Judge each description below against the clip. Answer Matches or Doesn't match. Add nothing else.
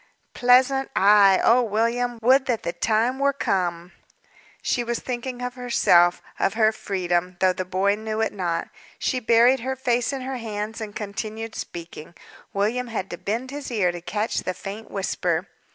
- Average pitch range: Matches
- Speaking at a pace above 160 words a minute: Matches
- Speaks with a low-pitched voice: Doesn't match